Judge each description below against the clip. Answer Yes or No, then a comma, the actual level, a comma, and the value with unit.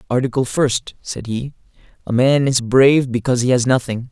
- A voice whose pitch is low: Yes, low, 125 Hz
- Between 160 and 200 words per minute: Yes, average, 175 wpm